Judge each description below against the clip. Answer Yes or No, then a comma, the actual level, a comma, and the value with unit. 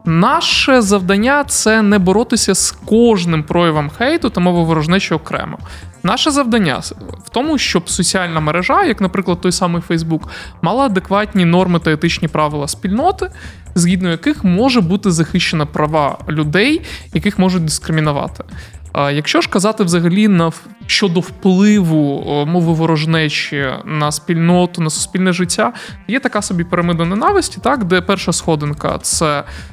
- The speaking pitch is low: No, medium, 180 Hz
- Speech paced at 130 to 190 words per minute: Yes, average, 135 wpm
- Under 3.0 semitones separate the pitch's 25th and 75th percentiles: No, average, 4.7 semitones